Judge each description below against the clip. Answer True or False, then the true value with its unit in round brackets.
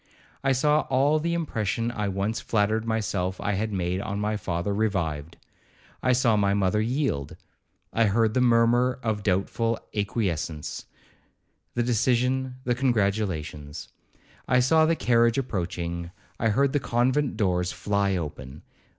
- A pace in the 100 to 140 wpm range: True (135 wpm)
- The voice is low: True (110 Hz)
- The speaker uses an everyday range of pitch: True (4.8 semitones)